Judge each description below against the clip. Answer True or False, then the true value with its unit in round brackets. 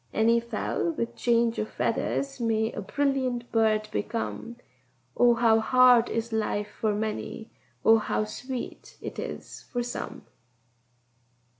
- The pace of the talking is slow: True (130 wpm)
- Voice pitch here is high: True (230 Hz)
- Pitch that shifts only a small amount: True (1.7 semitones)